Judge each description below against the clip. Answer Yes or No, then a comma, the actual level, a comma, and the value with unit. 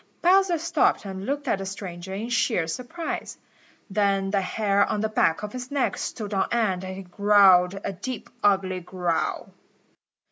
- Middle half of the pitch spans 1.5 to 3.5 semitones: No, average, 4.0 semitones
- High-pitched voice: Yes, high, 200 Hz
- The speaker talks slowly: No, average, 170 wpm